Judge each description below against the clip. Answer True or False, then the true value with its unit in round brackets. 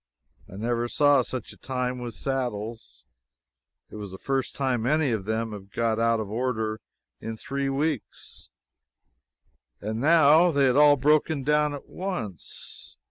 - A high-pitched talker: False (125 Hz)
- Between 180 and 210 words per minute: False (150 wpm)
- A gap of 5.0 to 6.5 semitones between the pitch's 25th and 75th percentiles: False (4.4 semitones)